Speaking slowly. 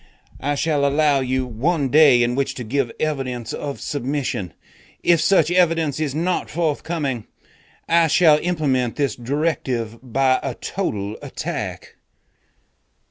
Yes: slow, 130 wpm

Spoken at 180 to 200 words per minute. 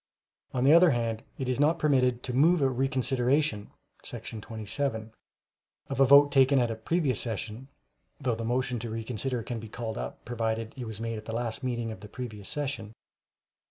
Yes: average, 190 wpm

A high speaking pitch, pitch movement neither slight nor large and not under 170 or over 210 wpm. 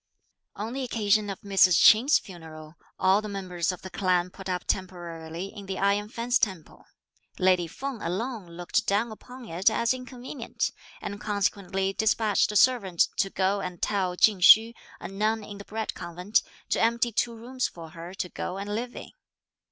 Yes: high, 200 Hz; average, 3.5 semitones; average, 175 wpm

